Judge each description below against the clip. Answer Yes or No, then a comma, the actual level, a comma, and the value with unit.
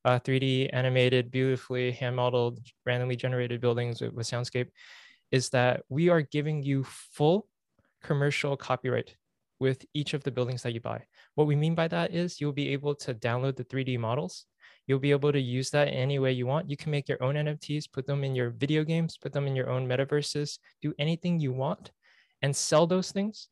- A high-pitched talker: No, low, 135 Hz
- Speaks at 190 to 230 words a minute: Yes, average, 200 wpm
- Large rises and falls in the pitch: No, average, 2.9 semitones